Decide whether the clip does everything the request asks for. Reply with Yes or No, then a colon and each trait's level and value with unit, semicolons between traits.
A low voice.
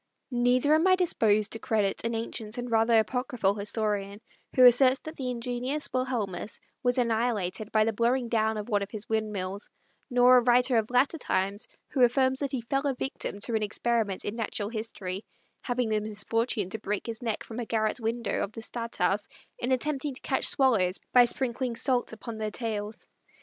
No: high, 230 Hz